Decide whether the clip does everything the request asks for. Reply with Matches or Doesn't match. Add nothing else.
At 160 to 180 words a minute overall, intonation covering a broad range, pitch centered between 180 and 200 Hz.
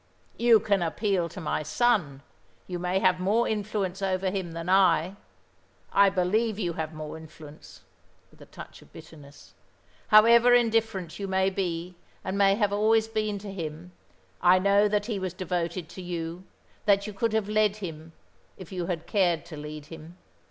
Doesn't match